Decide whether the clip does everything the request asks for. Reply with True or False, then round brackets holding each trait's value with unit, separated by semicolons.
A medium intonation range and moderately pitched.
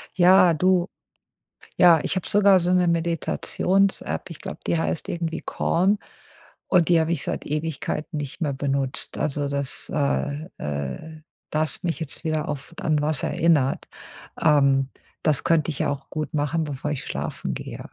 True (3.3 semitones; 155 Hz)